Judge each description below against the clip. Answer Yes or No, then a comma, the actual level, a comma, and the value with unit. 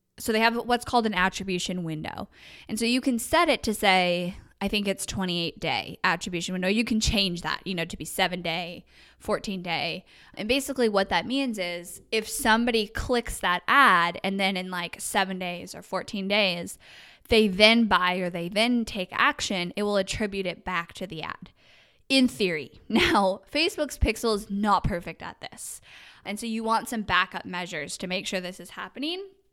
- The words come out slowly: No, average, 185 wpm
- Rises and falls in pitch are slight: No, average, 4.1 semitones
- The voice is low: No, high, 195 Hz